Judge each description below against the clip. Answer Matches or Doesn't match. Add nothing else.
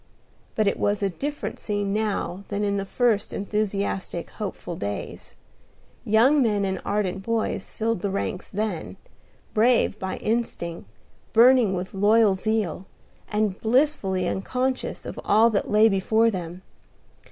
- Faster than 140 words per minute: Doesn't match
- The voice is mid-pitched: Doesn't match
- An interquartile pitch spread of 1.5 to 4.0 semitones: Matches